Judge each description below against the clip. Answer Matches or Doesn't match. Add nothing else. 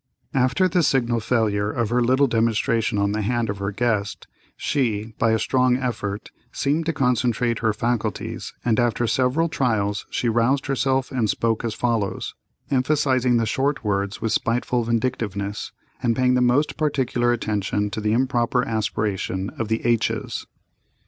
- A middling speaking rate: Matches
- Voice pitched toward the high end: Doesn't match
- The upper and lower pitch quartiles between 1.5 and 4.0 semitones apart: Matches